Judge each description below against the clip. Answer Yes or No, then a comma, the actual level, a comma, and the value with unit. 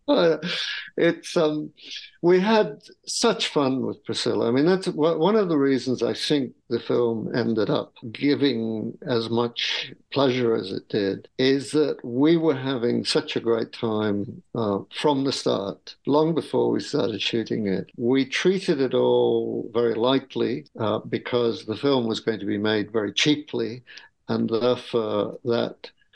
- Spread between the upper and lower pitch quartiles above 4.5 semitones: Yes, average, 4.9 semitones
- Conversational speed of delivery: Yes, average, 155 wpm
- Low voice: Yes, low, 125 Hz